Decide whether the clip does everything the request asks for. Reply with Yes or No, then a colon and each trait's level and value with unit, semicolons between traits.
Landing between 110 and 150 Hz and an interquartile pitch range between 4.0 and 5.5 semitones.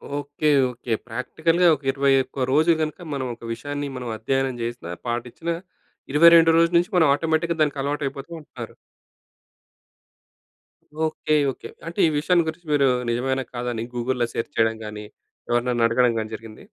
Yes: low, 135 Hz; average, 4.5 semitones